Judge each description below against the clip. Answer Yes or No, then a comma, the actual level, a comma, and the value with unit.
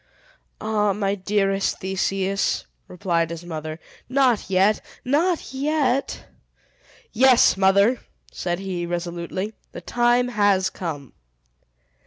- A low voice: No, high, 195 Hz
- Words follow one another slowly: Yes, slow, 100 wpm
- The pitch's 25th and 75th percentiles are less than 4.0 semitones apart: No, average, 5.0 semitones